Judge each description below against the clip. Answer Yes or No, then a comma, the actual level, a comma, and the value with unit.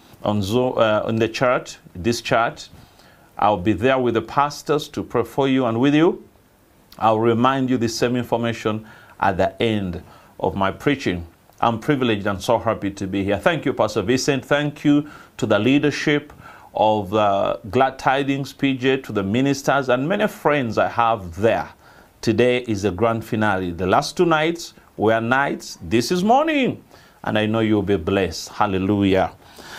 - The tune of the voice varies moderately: Yes, average, 4.8 semitones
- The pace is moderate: Yes, average, 175 wpm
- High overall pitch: No, low, 115 Hz